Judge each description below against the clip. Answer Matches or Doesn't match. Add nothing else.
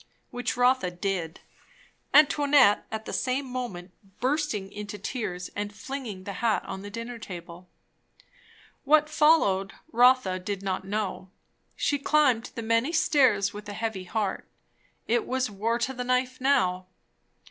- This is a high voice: Matches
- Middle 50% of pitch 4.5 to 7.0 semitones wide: Matches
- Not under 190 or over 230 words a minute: Doesn't match